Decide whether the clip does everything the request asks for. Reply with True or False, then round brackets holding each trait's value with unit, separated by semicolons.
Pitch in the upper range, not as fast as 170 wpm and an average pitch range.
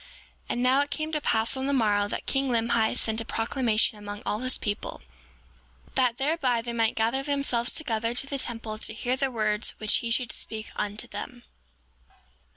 False (235 Hz; 190 wpm; 3.2 semitones)